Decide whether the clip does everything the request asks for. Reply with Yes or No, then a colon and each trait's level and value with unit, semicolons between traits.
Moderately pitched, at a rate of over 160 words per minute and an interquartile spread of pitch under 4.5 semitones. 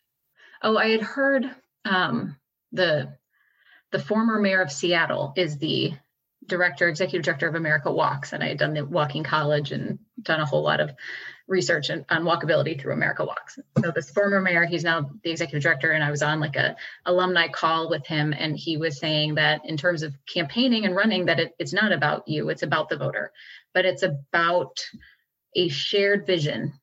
Yes: medium, 170 Hz; average, 190 wpm; average, 3.2 semitones